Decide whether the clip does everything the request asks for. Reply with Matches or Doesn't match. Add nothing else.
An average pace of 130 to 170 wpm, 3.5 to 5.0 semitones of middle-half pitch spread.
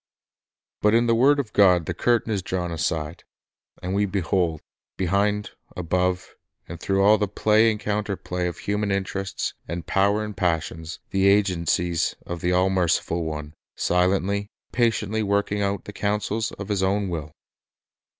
Doesn't match